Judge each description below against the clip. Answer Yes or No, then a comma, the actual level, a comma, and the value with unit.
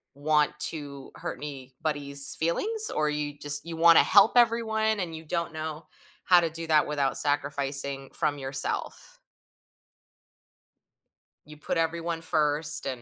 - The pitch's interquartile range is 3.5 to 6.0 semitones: No, narrow, 2.6 semitones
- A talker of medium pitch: Yes, medium, 150 Hz